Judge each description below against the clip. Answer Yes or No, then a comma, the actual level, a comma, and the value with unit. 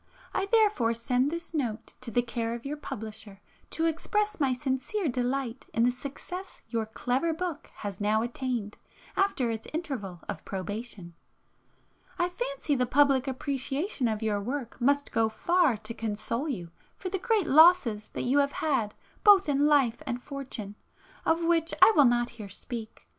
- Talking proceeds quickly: No, average, 165 wpm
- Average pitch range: No, wide, 5.8 semitones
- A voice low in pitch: No, very high, 260 Hz